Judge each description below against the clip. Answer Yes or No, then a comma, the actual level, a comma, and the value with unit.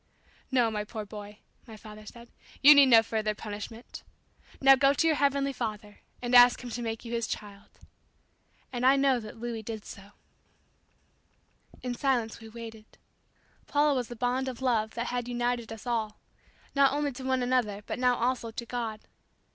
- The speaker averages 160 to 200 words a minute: Yes, average, 180 wpm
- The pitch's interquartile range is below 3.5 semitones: Yes, average, 2.8 semitones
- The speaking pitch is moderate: No, high, 240 Hz